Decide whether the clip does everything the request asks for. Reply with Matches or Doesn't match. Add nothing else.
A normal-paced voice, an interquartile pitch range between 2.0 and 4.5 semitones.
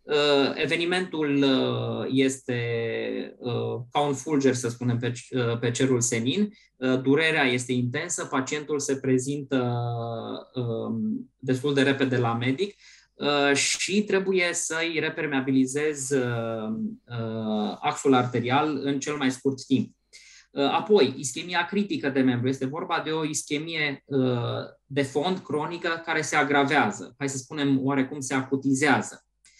Doesn't match